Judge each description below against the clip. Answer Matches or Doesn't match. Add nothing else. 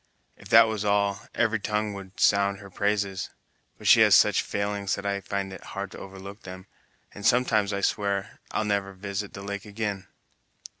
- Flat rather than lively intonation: Matches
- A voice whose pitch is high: Doesn't match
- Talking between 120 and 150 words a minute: Doesn't match